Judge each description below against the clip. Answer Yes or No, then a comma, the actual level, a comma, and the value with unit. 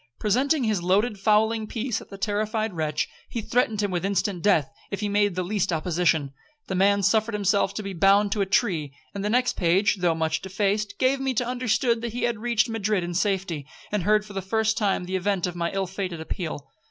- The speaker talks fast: Yes, fast, 215 wpm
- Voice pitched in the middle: No, high, 200 Hz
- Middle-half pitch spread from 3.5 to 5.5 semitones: No, average, 3.0 semitones